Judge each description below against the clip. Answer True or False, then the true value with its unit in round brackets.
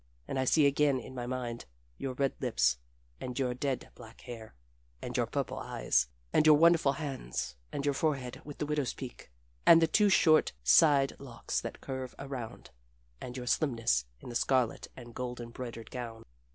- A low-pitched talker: True (130 Hz)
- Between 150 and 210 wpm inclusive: True (180 wpm)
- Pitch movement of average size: True (3.1 semitones)